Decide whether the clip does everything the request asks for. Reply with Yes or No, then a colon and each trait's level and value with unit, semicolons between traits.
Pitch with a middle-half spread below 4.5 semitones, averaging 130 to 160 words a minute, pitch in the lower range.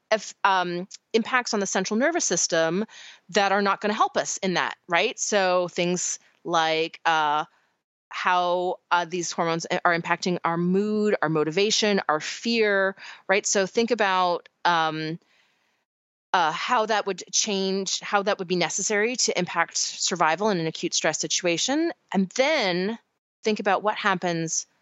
No: average, 3.5 semitones; average, 150 wpm; high, 190 Hz